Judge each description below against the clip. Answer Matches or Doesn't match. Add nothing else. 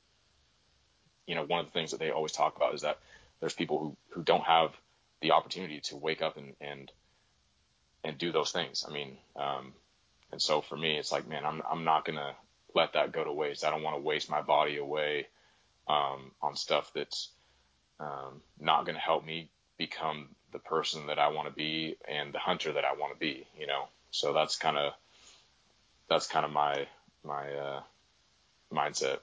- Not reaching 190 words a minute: Doesn't match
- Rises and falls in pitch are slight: Matches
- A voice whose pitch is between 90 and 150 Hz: Doesn't match